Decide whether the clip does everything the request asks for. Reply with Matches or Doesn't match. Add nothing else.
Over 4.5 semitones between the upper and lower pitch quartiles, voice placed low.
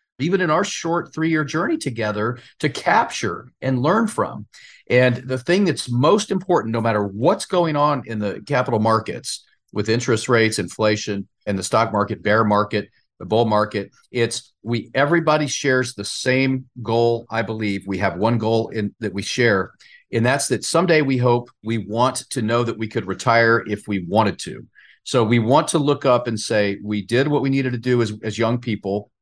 Doesn't match